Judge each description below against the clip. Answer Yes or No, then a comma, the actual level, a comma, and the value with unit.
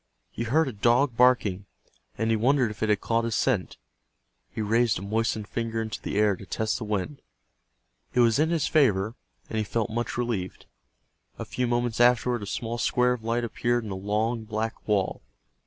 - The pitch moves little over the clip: Yes, narrow, 2.3 semitones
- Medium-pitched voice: No, low, 115 Hz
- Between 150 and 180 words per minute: No, average, 195 wpm